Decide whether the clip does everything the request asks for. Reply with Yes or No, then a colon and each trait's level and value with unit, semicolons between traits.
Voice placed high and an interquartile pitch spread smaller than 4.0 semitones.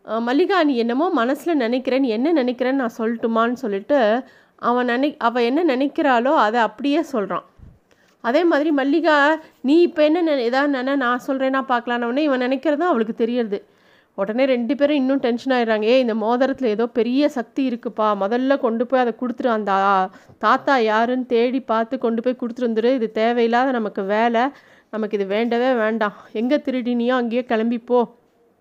Yes: high, 245 Hz; average, 2.9 semitones